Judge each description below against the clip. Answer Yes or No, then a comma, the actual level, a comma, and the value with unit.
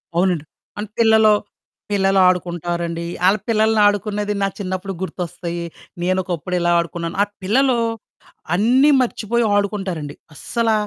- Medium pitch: No, high, 195 Hz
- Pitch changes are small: No, average, 3.7 semitones